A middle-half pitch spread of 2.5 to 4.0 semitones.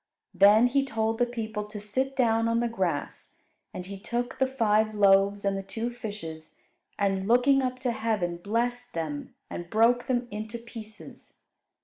Yes: average, 3.3 semitones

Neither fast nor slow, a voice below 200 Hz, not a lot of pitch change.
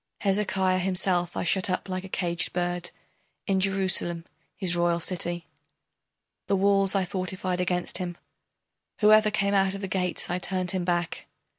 Yes: average, 155 wpm; medium, 185 Hz; narrow, 1.7 semitones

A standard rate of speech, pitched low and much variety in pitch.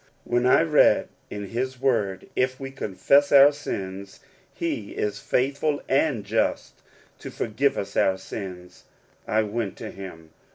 Yes: average, 150 wpm; low, 115 Hz; wide, 5.7 semitones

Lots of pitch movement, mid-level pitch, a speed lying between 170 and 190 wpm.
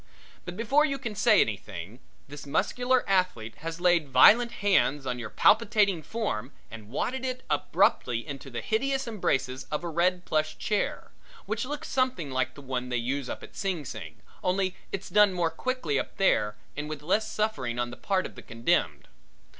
Yes: wide, 8.6 semitones; medium, 175 Hz; average, 180 wpm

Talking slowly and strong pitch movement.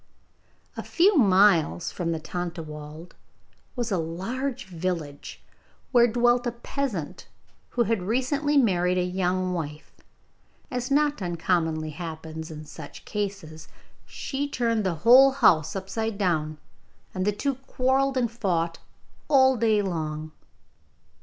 Yes: slow, 125 wpm; wide, 6.8 semitones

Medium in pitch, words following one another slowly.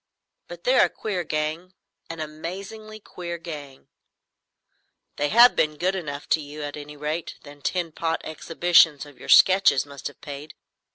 No: medium, 155 Hz; average, 155 wpm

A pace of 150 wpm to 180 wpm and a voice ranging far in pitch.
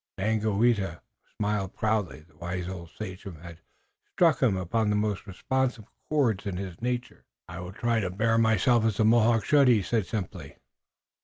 No: average, 160 wpm; average, 3.6 semitones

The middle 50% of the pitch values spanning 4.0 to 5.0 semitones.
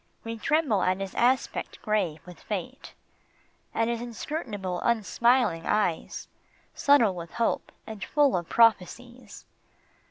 Yes: average, 4.5 semitones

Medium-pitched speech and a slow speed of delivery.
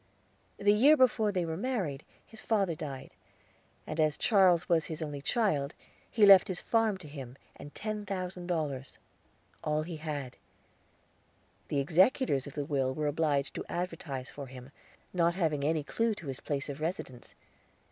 No: medium, 160 Hz; average, 165 wpm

